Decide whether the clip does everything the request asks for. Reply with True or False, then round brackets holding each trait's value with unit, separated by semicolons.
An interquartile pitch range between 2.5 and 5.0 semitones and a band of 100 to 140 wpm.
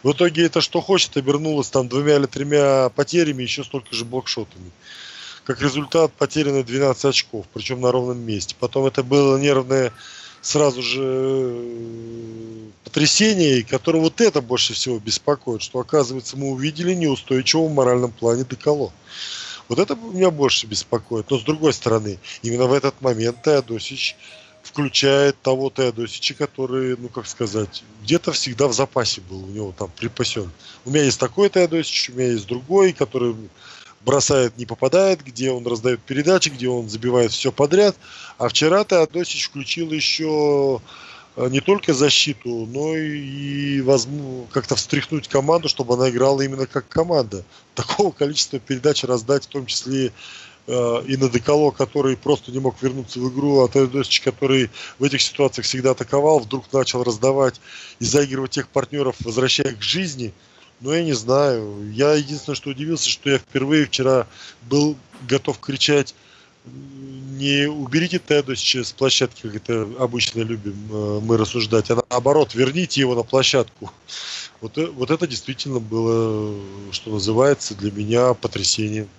False (3.3 semitones; 150 wpm)